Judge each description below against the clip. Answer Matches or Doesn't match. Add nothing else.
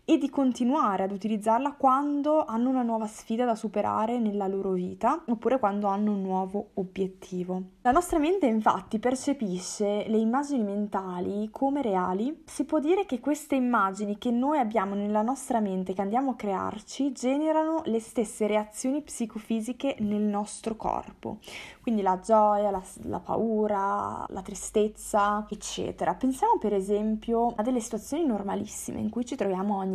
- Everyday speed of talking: Matches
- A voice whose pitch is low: Doesn't match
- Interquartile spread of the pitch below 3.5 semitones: Doesn't match